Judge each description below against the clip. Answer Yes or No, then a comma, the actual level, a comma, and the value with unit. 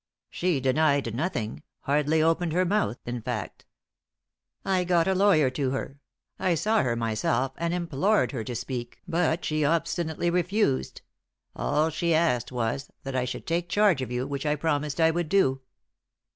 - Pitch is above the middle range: No, medium, 155 Hz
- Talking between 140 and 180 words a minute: Yes, average, 165 wpm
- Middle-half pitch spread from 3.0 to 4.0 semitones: No, average, 4.9 semitones